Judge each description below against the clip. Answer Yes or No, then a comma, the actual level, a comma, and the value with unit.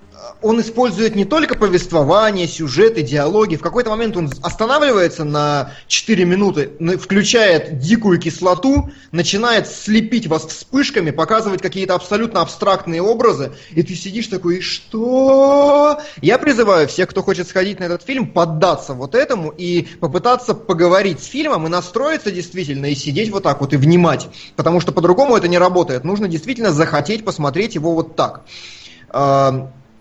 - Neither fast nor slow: Yes, average, 145 wpm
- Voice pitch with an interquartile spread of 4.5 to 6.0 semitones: Yes, average, 5.2 semitones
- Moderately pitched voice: Yes, medium, 180 Hz